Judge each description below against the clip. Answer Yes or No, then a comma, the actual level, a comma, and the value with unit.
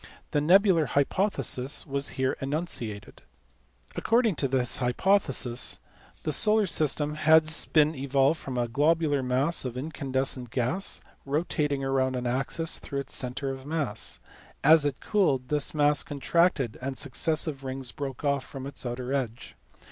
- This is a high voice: No, medium, 140 Hz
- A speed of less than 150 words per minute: Yes, average, 140 wpm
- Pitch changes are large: No, average, 3.1 semitones